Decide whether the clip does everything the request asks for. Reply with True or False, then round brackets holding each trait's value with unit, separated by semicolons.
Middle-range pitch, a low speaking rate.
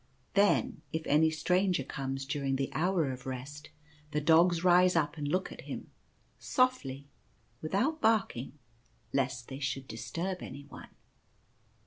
True (150 Hz; 130 wpm)